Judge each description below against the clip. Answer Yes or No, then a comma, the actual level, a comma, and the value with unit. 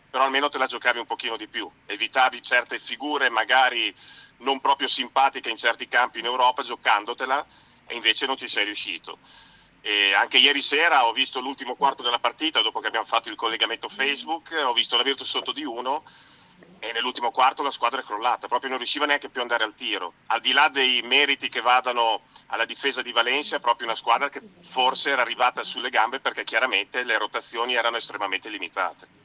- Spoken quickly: Yes, fast, 195 wpm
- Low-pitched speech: Yes, low, 130 Hz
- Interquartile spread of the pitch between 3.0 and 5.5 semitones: No, narrow, 2.6 semitones